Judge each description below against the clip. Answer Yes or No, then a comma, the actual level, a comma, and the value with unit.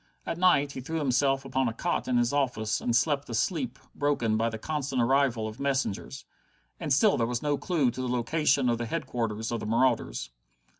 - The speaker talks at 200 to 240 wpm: Yes, fast, 205 wpm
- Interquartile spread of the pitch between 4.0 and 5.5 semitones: No, average, 3.5 semitones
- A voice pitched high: No, low, 130 Hz